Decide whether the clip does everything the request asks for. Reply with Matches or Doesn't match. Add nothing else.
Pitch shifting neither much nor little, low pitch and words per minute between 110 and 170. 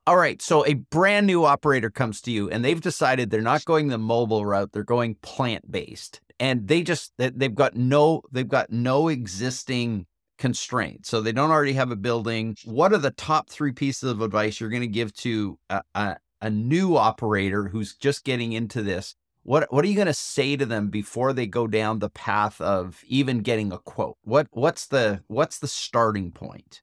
Doesn't match